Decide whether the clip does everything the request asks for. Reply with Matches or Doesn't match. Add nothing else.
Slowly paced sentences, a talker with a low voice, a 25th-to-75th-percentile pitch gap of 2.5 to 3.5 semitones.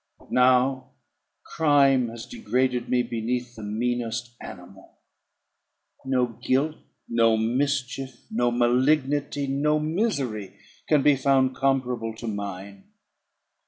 Matches